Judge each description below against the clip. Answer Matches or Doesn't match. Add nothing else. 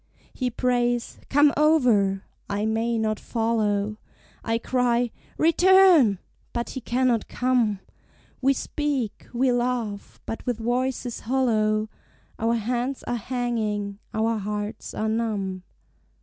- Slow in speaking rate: Matches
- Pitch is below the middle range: Doesn't match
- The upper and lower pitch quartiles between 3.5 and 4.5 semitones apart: Doesn't match